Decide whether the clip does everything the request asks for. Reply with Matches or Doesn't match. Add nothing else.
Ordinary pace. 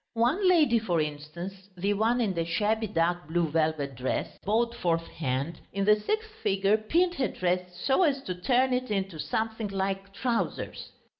Matches